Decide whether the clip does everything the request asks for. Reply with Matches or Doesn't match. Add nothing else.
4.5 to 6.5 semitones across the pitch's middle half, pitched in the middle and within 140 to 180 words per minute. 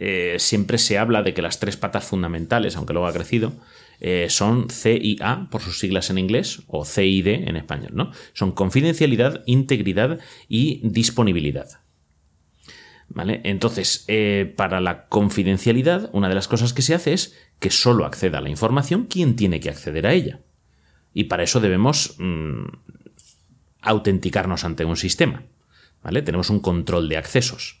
Doesn't match